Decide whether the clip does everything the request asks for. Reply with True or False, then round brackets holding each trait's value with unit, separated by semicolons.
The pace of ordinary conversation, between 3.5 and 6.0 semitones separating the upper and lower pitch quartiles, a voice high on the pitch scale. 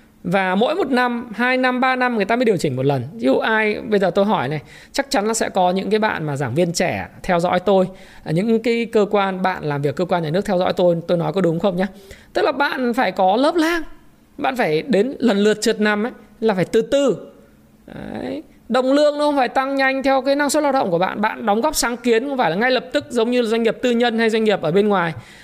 False (275 wpm; 5.1 semitones; 220 Hz)